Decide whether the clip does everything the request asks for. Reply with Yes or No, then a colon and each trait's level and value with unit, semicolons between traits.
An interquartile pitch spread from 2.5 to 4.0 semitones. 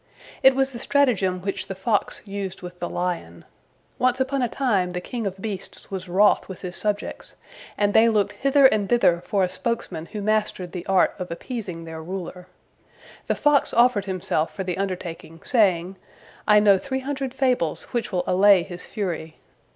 No: average, 4.7 semitones